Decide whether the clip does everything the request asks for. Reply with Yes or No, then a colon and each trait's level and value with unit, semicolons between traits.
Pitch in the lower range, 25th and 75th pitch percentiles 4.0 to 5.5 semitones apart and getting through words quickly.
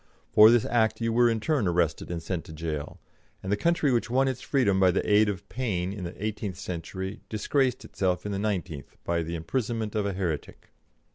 Yes: low, 100 Hz; average, 4.6 semitones; fast, 210 wpm